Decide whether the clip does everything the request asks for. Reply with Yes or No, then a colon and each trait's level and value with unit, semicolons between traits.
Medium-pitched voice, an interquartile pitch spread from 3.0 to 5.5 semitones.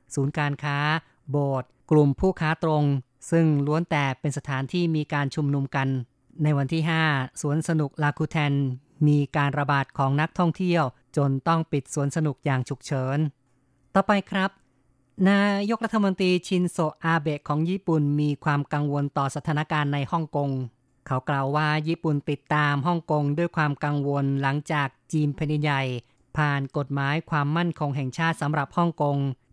No: medium, 145 Hz; narrow, 2.4 semitones